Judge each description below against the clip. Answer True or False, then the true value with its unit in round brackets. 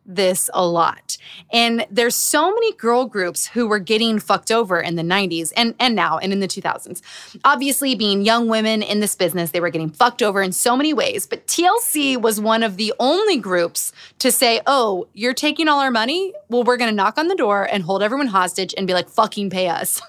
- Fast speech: True (220 wpm)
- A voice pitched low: False (225 Hz)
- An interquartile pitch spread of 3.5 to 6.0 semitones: True (4.8 semitones)